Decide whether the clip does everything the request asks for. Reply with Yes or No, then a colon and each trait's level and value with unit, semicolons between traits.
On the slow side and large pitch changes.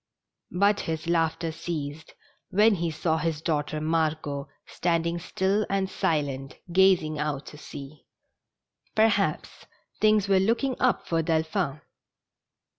No: slow, 125 wpm; average, 3.8 semitones